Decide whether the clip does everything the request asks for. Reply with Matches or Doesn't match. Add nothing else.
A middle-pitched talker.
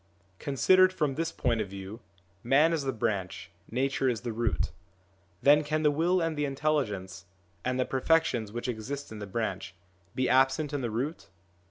Doesn't match